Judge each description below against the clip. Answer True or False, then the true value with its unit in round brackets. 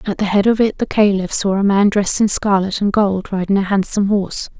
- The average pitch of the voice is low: False (200 Hz)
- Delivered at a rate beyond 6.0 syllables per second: False (5.9 syllables/s)